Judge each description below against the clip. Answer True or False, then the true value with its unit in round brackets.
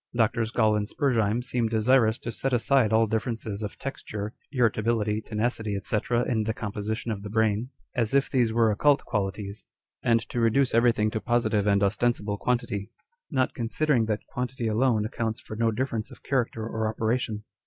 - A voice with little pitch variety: True (2.2 semitones)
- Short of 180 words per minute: True (170 wpm)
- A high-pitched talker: False (110 Hz)